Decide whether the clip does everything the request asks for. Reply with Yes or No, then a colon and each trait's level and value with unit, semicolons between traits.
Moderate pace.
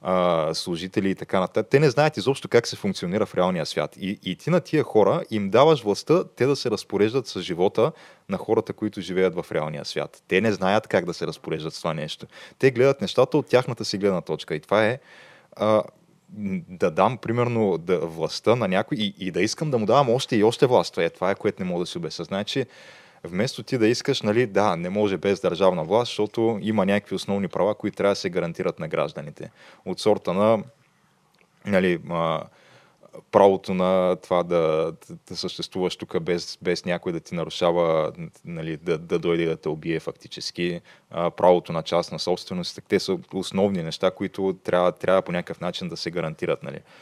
No: fast, 195 wpm